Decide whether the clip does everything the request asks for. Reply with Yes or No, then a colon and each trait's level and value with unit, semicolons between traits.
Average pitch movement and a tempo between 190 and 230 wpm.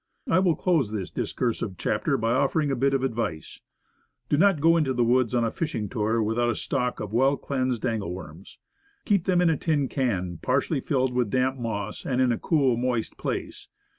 Yes: average, 3.9 semitones; average, 200 wpm